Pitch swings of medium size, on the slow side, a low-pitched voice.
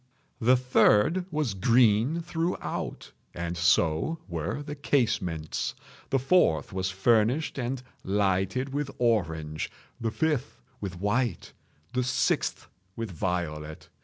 No: wide, 7.0 semitones; slow, 105 wpm; low, 110 Hz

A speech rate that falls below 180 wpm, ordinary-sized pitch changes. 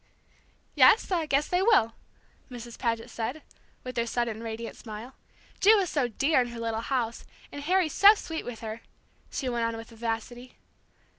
Yes: average, 170 wpm; average, 4.8 semitones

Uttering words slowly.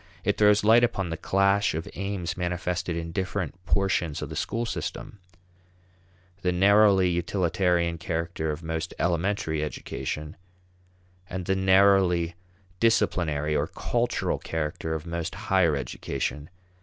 Yes: slow, 125 wpm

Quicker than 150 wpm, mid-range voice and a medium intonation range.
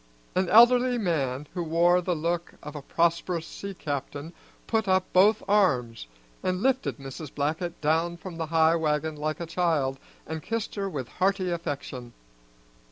Yes: average, 160 wpm; medium, 170 Hz; average, 3.7 semitones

